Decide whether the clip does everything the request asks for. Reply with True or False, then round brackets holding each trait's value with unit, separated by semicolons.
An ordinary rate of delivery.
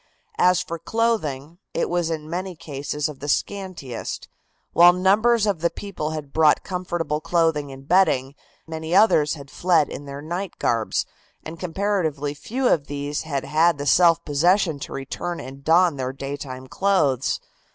True (160 wpm)